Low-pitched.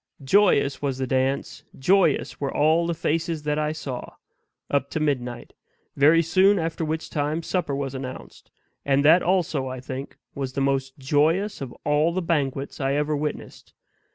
No: medium, 145 Hz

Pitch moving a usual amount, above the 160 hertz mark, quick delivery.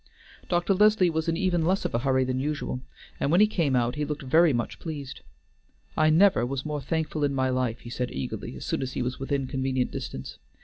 No: average, 4.3 semitones; medium, 140 Hz; fast, 225 wpm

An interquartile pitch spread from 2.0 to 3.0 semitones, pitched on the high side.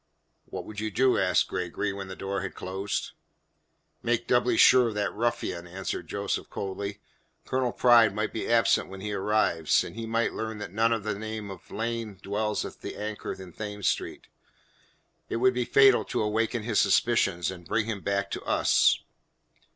No: average, 2.7 semitones; low, 105 Hz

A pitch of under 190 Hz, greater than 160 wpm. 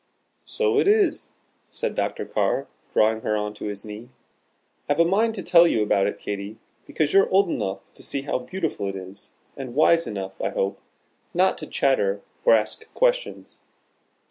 Yes: low, 135 Hz; average, 175 wpm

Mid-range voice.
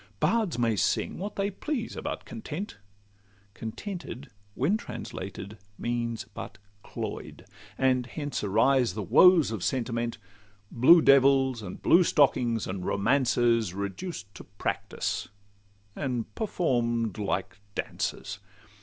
No: low, 120 Hz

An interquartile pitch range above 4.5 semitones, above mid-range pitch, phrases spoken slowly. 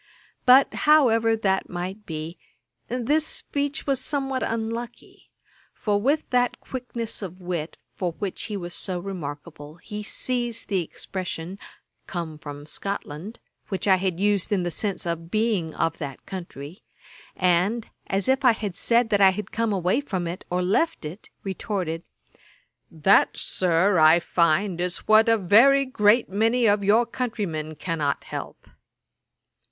No: average, 4.9 semitones; high, 195 Hz; average, 145 wpm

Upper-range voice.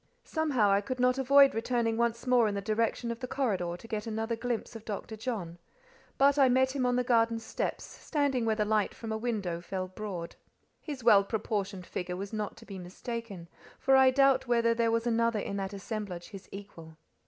Yes: high, 225 Hz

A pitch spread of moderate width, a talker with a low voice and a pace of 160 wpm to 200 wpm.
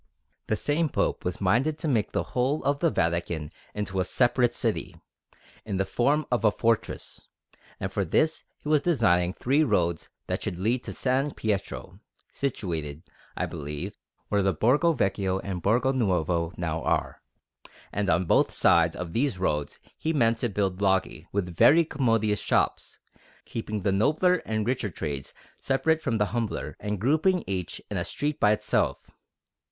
No: wide, 6.6 semitones; low, 105 Hz; average, 170 wpm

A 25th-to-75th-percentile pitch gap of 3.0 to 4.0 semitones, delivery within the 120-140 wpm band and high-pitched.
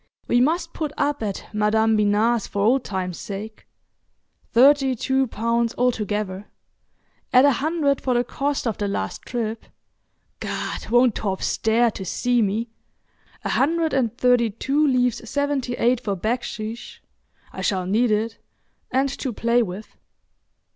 Yes: average, 3.7 semitones; slow, 135 wpm; high, 235 Hz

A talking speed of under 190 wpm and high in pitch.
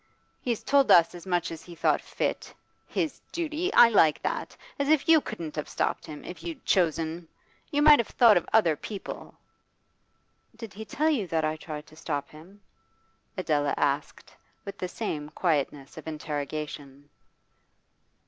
No: average, 160 wpm; medium, 170 Hz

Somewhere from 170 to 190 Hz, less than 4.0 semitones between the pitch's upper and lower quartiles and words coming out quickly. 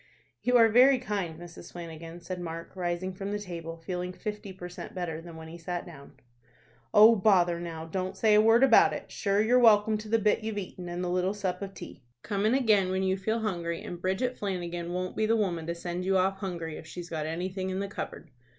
Yes: medium, 185 Hz; average, 3.3 semitones; fast, 230 wpm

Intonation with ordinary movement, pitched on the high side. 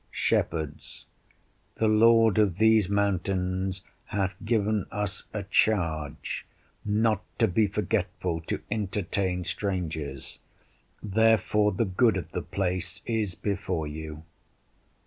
No: average, 3.1 semitones; low, 100 Hz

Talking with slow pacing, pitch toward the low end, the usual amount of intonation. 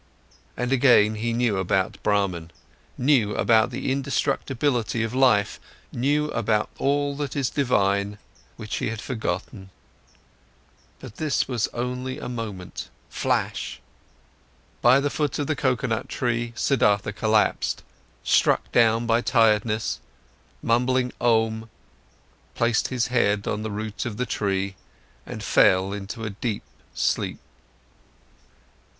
Yes: slow, 120 wpm; low, 115 Hz; average, 3.4 semitones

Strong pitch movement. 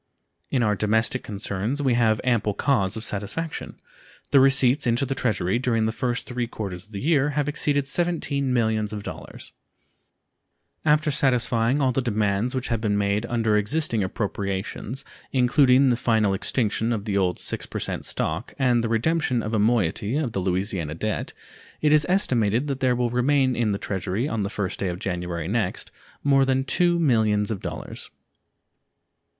No: average, 4.4 semitones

